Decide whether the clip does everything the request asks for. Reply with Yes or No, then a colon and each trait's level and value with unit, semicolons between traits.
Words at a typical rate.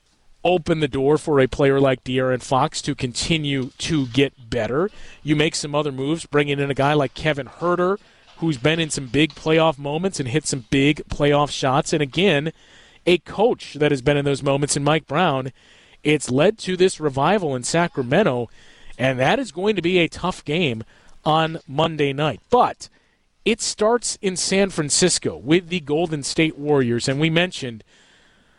Yes: average, 180 wpm